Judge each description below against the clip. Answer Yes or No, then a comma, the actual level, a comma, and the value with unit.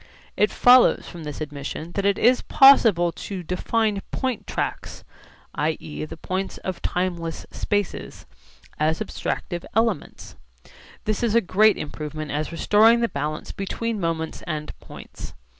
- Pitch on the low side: No, medium, 185 Hz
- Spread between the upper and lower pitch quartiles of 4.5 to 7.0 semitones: Yes, wide, 5.5 semitones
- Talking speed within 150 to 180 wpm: No, slow, 135 wpm